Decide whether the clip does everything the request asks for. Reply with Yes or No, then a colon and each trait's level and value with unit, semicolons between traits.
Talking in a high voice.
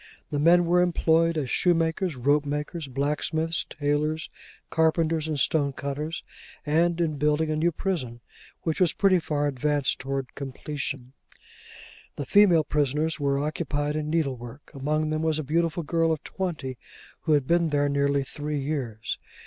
No: medium, 150 Hz